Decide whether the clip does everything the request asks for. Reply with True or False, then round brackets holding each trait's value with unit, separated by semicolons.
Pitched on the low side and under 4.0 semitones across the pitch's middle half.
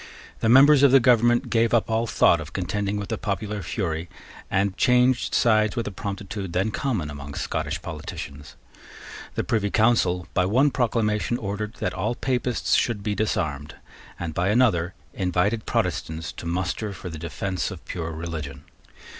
False (100 Hz; 5.1 semitones)